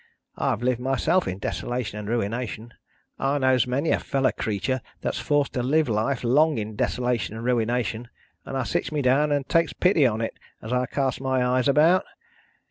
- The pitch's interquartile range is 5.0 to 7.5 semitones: No, average, 3.2 semitones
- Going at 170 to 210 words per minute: Yes, average, 185 wpm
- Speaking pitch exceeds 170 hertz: No, low, 125 Hz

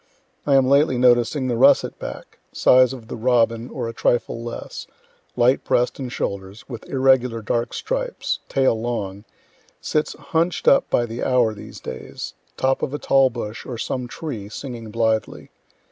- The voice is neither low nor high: No, low, 120 Hz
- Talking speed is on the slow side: No, average, 160 wpm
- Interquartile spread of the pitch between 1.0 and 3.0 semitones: Yes, narrow, 2.6 semitones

